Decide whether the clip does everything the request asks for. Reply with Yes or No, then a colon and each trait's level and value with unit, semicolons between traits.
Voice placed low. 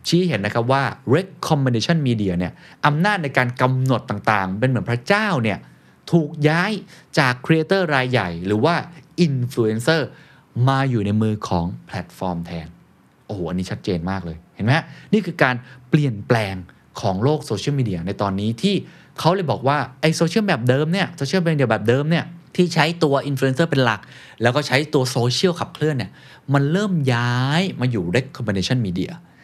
Yes: low, 130 Hz